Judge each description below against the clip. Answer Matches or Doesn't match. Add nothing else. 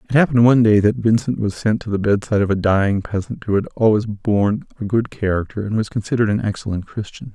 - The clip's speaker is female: Doesn't match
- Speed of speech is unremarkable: Doesn't match